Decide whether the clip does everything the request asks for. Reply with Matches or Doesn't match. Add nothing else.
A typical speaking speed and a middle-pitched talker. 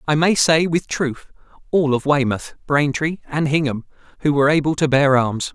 Matches